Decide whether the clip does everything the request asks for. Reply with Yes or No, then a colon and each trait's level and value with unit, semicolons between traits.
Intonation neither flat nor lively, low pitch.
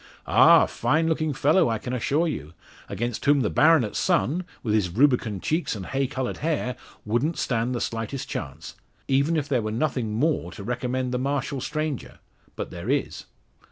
Yes: average, 4.8 semitones; low, 130 Hz